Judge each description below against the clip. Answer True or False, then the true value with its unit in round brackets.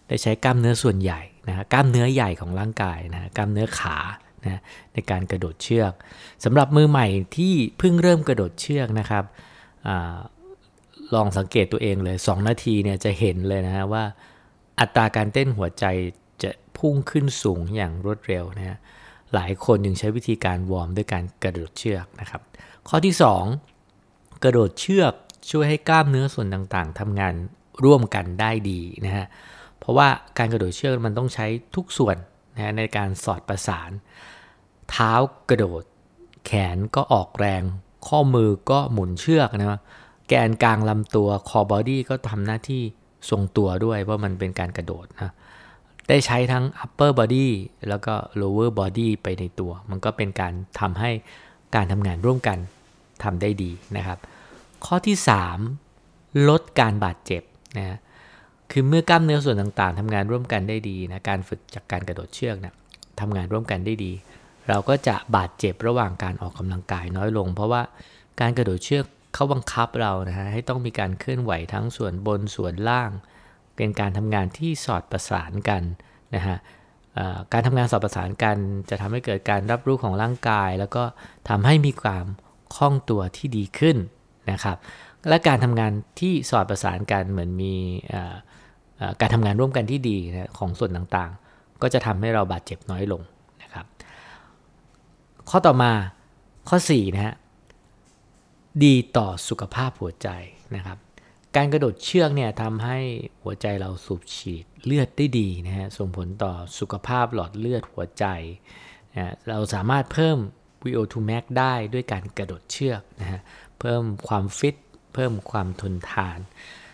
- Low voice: True (105 Hz)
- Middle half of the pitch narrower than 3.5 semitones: False (4.4 semitones)